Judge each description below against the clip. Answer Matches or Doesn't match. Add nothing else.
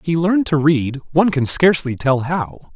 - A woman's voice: Doesn't match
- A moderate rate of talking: Matches